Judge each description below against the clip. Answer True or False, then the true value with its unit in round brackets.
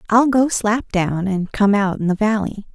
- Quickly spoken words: True (220 wpm)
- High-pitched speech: True (210 Hz)